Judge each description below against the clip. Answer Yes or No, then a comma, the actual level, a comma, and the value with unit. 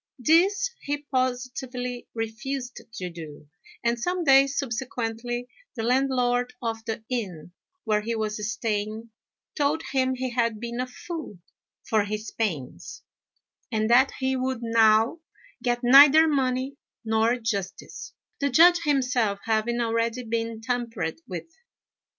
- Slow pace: Yes, slow, 125 wpm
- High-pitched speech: Yes, high, 240 Hz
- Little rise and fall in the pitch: No, average, 3.0 semitones